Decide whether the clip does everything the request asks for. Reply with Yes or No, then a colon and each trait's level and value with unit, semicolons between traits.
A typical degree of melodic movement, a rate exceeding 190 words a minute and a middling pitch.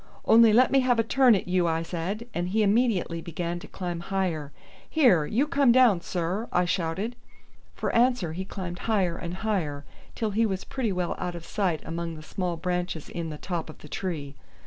Yes: average, 4.6 semitones; average, 200 wpm; medium, 180 Hz